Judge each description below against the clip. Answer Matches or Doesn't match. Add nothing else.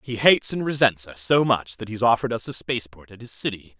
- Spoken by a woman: Doesn't match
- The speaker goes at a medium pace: Doesn't match